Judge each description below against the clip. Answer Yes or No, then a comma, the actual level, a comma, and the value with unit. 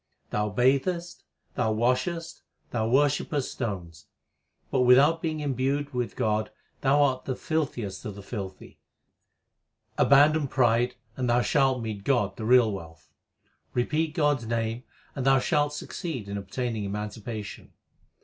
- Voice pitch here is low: Yes, low, 125 Hz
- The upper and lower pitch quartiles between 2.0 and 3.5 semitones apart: No, average, 4.8 semitones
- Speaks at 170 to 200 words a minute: No, slow, 135 wpm